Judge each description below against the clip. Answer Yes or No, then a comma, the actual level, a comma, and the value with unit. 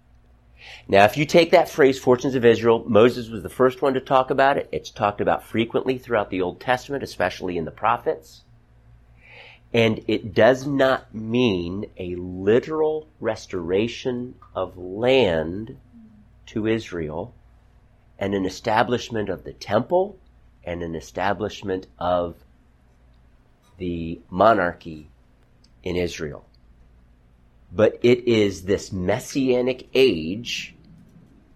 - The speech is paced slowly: Yes, slow, 120 wpm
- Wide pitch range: Yes, wide, 6.3 semitones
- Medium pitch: No, low, 105 Hz